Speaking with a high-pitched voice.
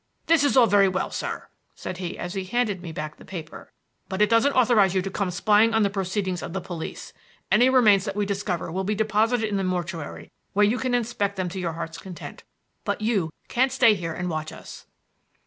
Yes: high, 195 Hz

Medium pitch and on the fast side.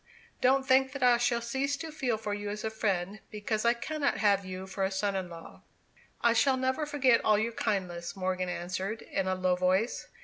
No: high, 215 Hz; fast, 210 wpm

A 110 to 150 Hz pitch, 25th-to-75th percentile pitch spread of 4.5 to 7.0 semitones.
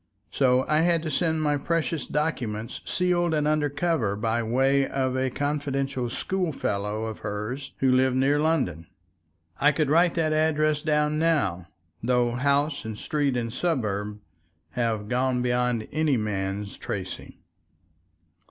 Yes: low, 135 Hz; average, 4.8 semitones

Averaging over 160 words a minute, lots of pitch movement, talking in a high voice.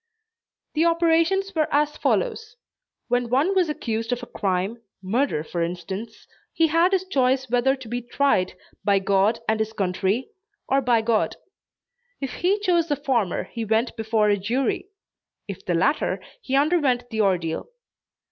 No: average, 155 wpm; wide, 6.2 semitones; high, 245 Hz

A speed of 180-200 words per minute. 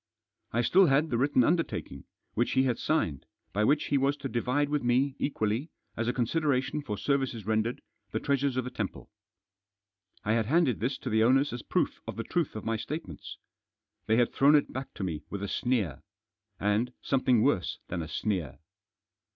Yes: average, 190 wpm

